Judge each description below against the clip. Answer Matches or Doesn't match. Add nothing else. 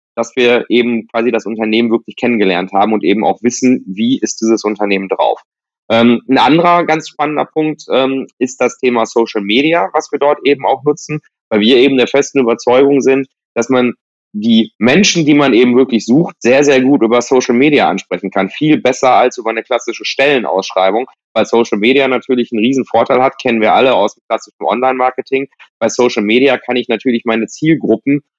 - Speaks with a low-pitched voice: Matches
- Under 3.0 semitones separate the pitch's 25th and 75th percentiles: Doesn't match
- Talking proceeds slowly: Doesn't match